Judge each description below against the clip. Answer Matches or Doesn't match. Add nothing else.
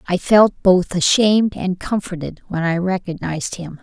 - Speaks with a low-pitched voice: Doesn't match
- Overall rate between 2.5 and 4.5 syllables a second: Doesn't match